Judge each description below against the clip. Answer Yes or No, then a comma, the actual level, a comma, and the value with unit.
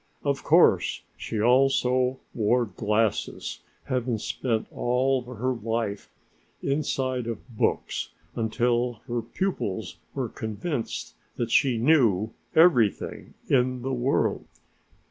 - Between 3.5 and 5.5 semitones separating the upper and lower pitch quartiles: No, narrow, 2.6 semitones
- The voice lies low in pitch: Yes, low, 120 Hz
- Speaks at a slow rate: Yes, slow, 105 wpm